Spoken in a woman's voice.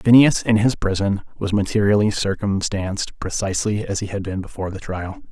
No: male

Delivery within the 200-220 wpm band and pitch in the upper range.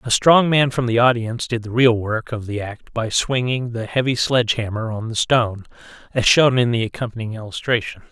No: fast, 205 wpm; low, 120 Hz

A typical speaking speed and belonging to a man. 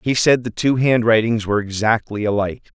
Yes: average, 170 wpm; male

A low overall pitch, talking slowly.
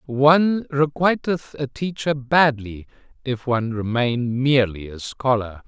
Yes: low, 130 Hz; slow, 115 wpm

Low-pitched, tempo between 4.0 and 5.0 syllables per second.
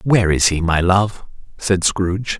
Yes: very low, 95 Hz; 4.4 syllables/s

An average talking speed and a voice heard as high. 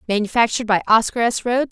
Yes: average, 175 wpm; high, 230 Hz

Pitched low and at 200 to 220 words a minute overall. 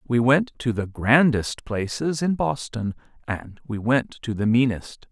No: low, 120 Hz; average, 165 wpm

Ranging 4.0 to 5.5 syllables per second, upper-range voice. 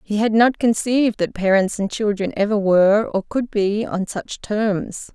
Yes: 4.5 syllables/s; high, 210 Hz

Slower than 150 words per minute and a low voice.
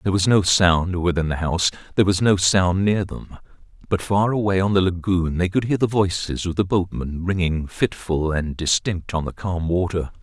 No: fast, 205 wpm; very low, 90 Hz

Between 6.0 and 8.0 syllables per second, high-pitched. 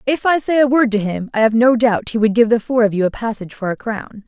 Yes: 6.1 syllables/s; high, 230 Hz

